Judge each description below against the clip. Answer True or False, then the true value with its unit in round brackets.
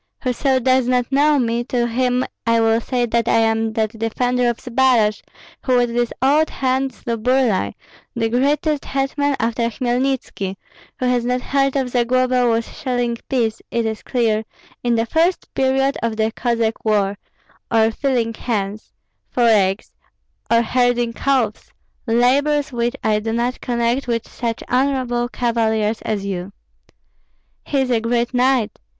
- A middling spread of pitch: False (2.2 semitones)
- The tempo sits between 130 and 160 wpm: True (155 wpm)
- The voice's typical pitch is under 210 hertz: False (240 Hz)